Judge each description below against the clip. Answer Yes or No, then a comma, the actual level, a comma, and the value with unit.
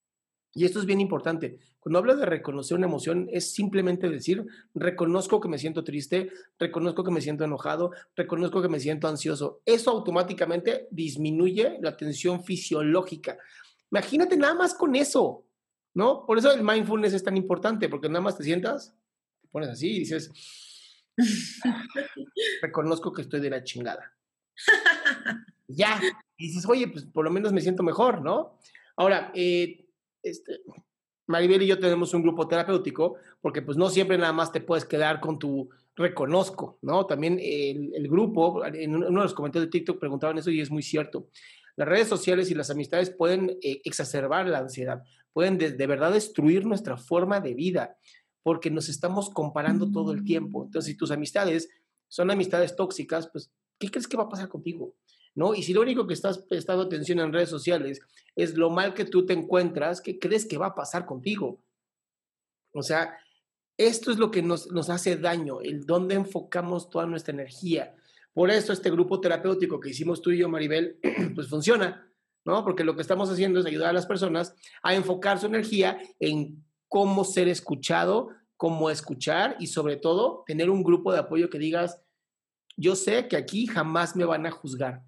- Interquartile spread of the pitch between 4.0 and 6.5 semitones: No, average, 3.3 semitones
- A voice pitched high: No, medium, 175 Hz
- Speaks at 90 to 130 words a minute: No, average, 180 wpm